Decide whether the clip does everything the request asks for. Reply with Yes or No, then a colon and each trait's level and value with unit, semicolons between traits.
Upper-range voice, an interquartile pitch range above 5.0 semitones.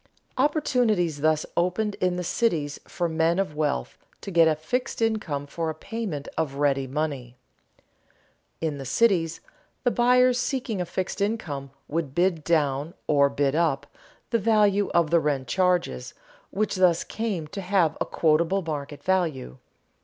No: medium, 170 Hz; wide, 5.5 semitones